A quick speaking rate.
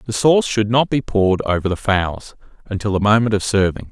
Yes: fast, 215 wpm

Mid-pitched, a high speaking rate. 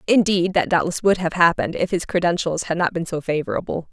Yes: medium, 175 Hz; fast, 215 wpm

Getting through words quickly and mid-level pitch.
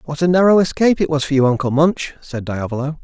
Yes: fast, 235 wpm; medium, 150 Hz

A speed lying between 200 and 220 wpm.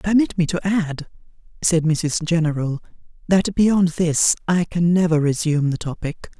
No: average, 150 wpm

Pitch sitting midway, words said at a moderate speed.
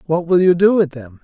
No: medium, 165 Hz; fast, 290 wpm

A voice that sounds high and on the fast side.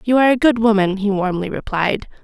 Yes: high, 215 Hz; fast, 215 wpm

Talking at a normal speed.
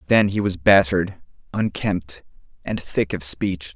Yes: average, 145 wpm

